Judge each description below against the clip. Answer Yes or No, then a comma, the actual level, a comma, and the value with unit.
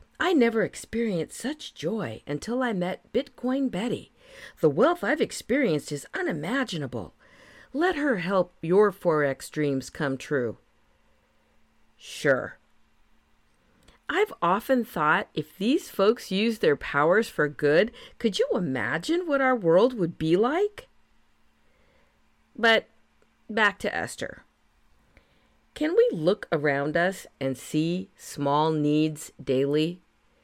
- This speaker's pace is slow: Yes, slow, 115 wpm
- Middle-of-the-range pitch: No, high, 195 Hz